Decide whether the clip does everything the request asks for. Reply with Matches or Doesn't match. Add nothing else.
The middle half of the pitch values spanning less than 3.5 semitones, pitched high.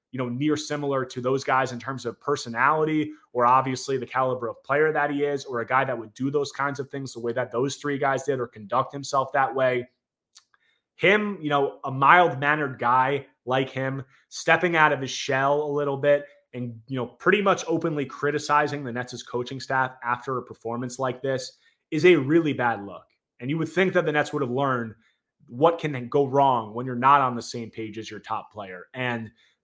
Doesn't match